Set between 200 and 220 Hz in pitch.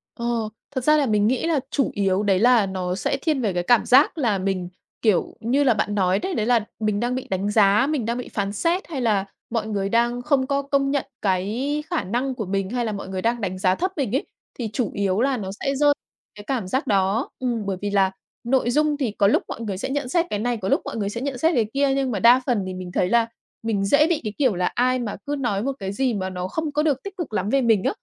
No: high, 230 Hz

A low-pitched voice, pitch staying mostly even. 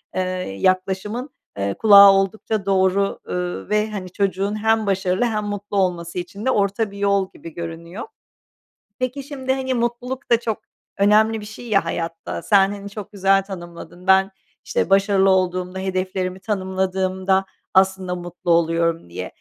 No: high, 195 Hz; narrow, 2.3 semitones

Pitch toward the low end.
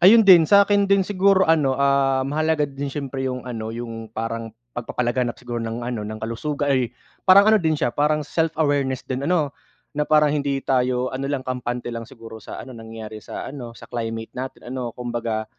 Yes: low, 130 Hz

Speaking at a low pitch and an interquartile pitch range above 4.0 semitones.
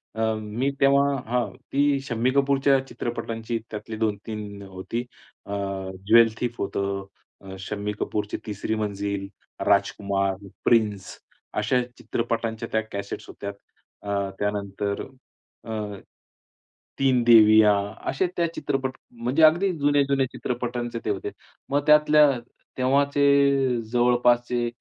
Yes: low, 115 Hz; average, 4.6 semitones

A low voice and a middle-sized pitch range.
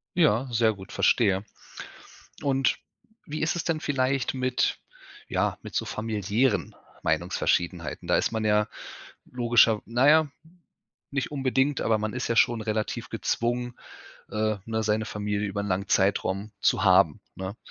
Yes: low, 110 Hz; average, 3.7 semitones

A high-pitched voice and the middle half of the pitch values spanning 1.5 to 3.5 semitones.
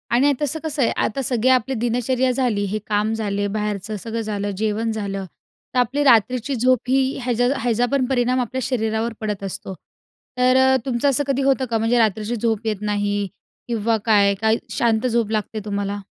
Yes: high, 230 Hz; average, 3.2 semitones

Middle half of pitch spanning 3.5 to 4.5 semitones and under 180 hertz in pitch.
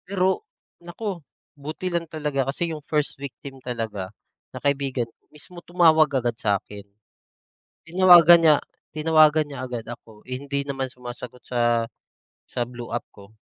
No: average, 4.9 semitones; medium, 140 Hz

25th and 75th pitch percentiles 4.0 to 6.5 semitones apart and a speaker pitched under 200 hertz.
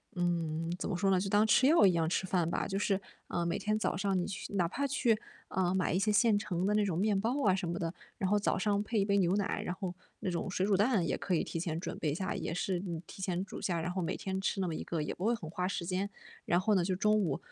No: average, 2.8 semitones; high, 190 Hz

